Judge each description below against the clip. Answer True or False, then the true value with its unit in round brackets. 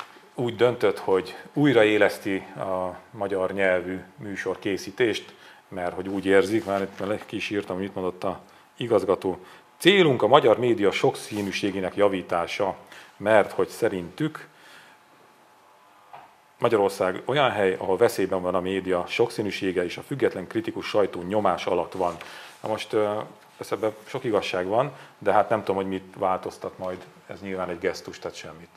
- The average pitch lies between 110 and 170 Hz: False (95 Hz)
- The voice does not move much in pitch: True (2.0 semitones)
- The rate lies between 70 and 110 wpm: False (140 wpm)